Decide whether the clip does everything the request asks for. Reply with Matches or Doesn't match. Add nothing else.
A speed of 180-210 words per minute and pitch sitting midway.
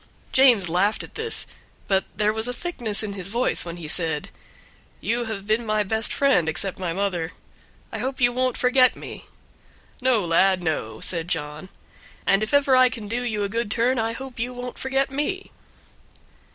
Doesn't match